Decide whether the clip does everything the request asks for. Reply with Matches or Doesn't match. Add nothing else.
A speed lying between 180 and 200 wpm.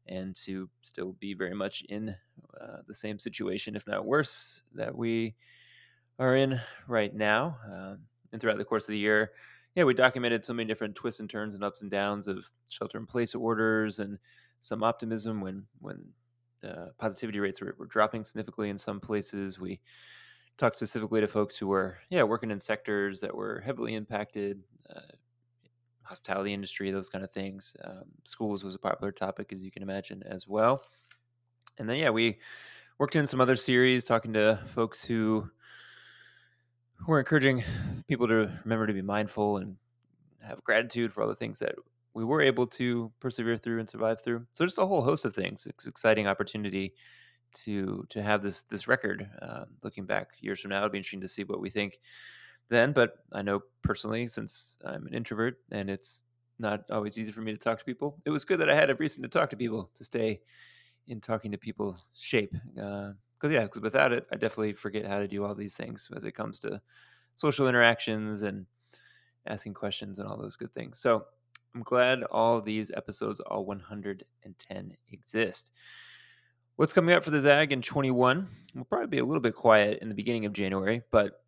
Matches